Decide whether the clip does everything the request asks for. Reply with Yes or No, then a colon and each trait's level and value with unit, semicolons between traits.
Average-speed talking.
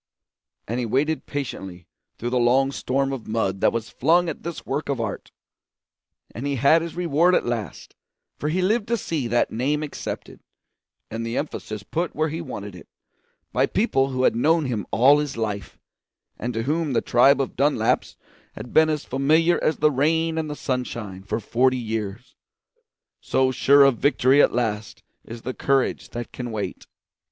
Yes: average, 180 wpm